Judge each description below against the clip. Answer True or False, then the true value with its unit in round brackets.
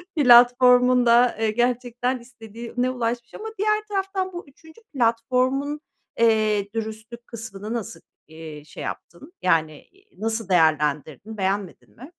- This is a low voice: False (235 Hz)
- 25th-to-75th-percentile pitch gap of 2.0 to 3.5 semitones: True (3.1 semitones)